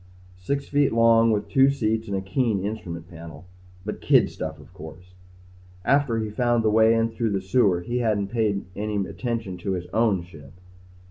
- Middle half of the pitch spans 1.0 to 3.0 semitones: No, average, 3.8 semitones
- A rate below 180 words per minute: No, average, 190 wpm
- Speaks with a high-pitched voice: No, low, 105 Hz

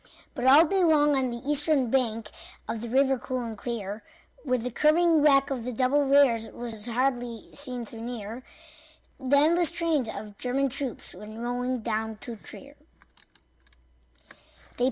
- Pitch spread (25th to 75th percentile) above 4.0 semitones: No, average, 3.6 semitones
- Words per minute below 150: No, average, 155 wpm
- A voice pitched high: Yes, very high, 250 Hz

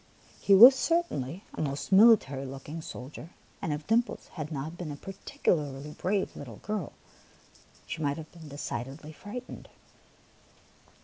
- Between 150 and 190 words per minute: No, slow, 135 wpm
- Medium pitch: Yes, medium, 155 Hz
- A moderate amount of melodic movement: No, wide, 5.7 semitones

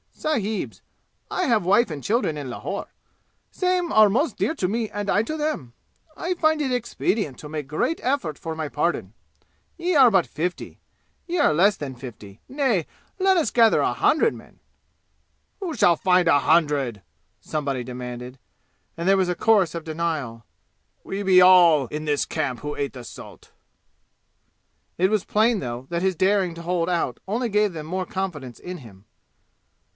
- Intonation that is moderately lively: No, wide, 7.1 semitones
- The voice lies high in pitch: No, medium, 180 Hz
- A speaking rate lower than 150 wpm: No, average, 175 wpm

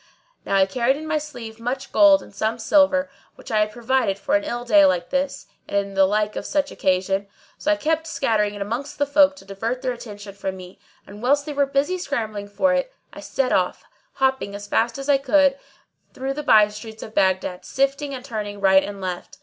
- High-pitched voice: Yes, high, 235 Hz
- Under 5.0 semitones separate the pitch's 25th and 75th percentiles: No, wide, 5.5 semitones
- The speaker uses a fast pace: Yes, fast, 215 wpm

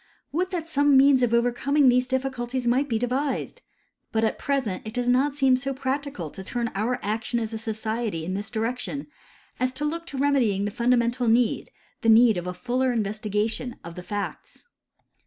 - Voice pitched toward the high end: Yes, high, 245 Hz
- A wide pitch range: No, average, 3.5 semitones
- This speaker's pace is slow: No, average, 195 wpm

